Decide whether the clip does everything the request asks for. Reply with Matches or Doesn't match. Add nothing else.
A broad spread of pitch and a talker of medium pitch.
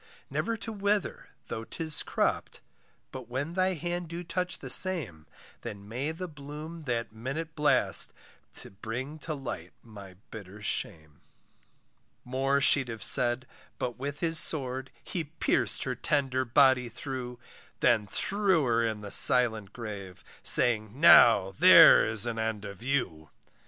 Doesn't match